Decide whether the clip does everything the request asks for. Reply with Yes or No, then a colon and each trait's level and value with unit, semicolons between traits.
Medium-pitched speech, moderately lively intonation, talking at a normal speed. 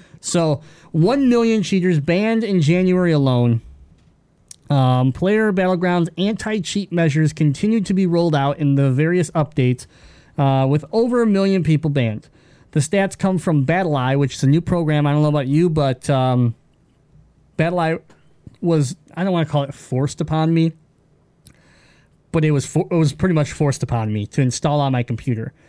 Yes: medium, 155 Hz; average, 4.1 semitones; average, 170 wpm